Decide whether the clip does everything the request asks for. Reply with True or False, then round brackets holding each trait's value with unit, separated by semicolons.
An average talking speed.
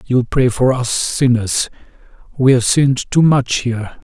True (160 wpm)